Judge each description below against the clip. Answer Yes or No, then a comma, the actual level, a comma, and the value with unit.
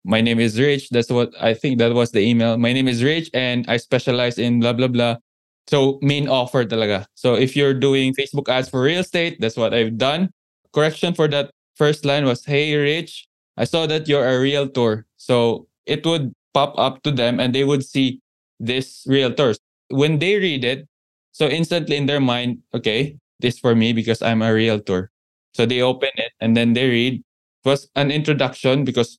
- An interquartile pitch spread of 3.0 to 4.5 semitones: Yes, average, 3.3 semitones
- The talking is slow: No, average, 200 wpm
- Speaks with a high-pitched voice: No, low, 130 Hz